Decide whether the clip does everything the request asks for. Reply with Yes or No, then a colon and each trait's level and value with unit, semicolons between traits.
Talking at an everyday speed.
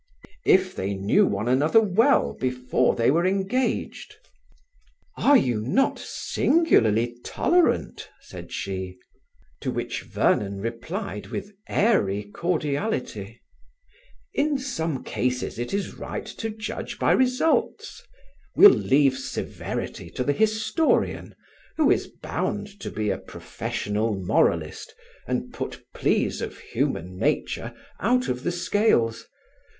No: slow, 115 wpm